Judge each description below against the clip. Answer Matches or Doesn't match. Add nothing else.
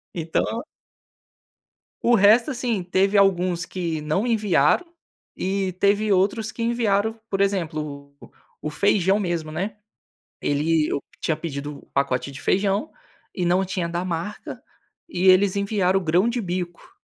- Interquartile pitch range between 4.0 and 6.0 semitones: Doesn't match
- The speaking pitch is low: Doesn't match